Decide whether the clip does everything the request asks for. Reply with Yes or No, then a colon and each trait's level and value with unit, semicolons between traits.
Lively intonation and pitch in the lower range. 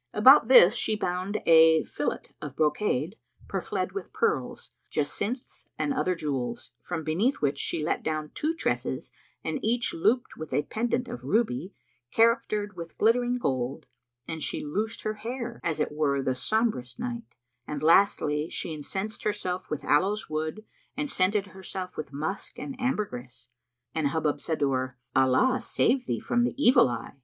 No: wide, 7.4 semitones; medium, 185 Hz